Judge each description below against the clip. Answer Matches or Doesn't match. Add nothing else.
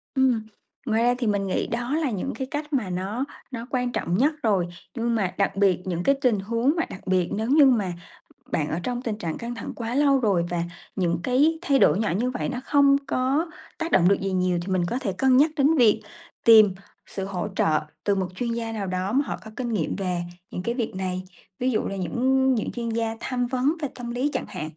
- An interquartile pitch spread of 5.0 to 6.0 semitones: Matches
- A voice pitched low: Doesn't match